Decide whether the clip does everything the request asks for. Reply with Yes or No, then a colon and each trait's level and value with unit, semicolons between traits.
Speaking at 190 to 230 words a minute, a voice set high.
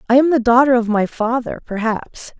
Yes: average, 200 wpm; high, 240 Hz